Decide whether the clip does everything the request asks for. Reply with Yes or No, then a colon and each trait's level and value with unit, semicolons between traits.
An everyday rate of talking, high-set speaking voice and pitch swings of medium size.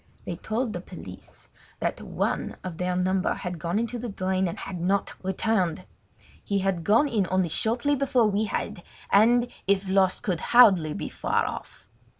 Yes: average, 170 wpm; high, 195 Hz; average, 3.6 semitones